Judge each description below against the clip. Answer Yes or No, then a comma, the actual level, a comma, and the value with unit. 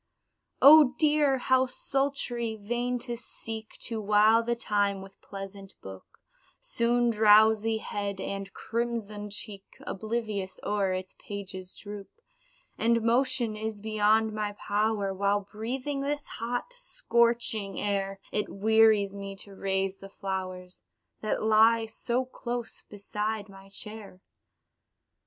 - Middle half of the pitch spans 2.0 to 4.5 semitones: Yes, average, 2.9 semitones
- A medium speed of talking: No, slow, 120 wpm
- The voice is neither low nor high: No, high, 215 Hz